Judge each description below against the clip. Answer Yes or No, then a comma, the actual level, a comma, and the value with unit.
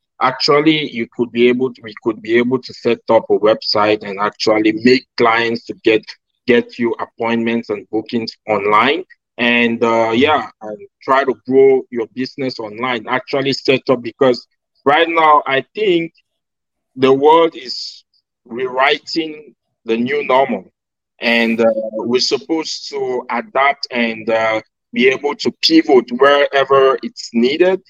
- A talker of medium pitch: No, low, 125 Hz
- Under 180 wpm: Yes, average, 145 wpm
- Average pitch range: Yes, average, 3.8 semitones